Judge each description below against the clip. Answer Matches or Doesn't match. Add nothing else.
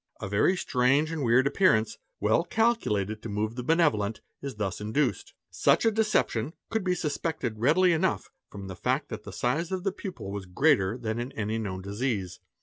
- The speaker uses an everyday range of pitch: Doesn't match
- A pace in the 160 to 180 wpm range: Doesn't match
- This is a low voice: Matches